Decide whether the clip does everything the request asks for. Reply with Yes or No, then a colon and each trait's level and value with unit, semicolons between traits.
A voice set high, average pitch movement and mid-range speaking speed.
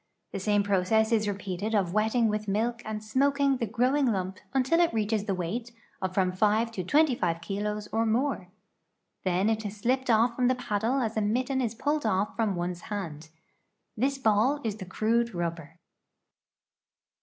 Yes: high, 215 Hz; average, 3.8 semitones; average, 180 wpm